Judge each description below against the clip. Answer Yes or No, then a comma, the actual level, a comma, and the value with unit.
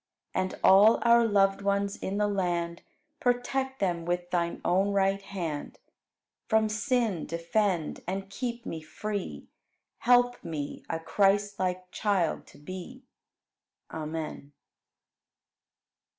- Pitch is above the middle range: Yes, high, 195 Hz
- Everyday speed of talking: No, slow, 110 wpm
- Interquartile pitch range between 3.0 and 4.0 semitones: Yes, average, 3.7 semitones